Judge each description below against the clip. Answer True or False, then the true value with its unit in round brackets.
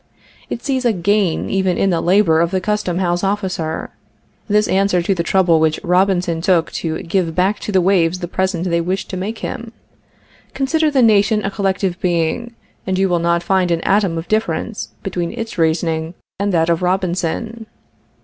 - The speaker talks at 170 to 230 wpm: True (185 wpm)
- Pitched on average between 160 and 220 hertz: True (185 Hz)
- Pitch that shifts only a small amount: False (3.0 semitones)